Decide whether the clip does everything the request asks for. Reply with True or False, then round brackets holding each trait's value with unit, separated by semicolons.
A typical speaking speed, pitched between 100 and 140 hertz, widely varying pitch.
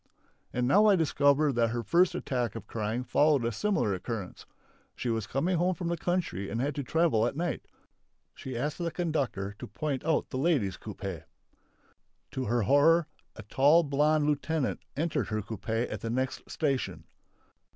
True (170 wpm; 135 Hz; 5.9 semitones)